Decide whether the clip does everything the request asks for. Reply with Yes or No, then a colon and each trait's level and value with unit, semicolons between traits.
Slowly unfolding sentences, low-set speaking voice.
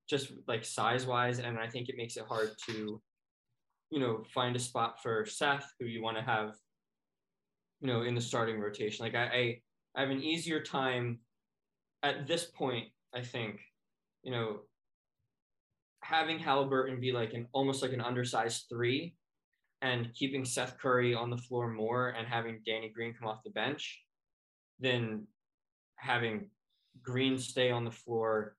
No: average, 160 wpm; low, 120 Hz